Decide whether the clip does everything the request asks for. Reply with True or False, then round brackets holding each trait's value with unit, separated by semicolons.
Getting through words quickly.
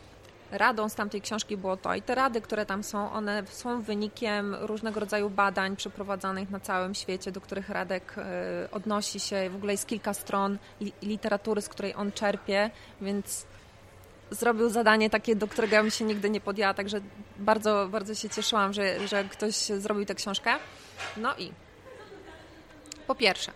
True (165 wpm)